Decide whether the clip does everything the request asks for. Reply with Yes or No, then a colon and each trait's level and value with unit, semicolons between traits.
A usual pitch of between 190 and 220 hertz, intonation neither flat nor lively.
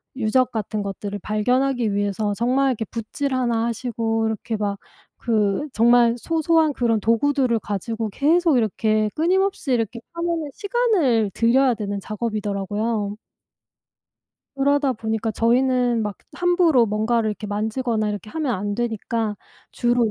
No: high, 230 Hz; average, 3.7 semitones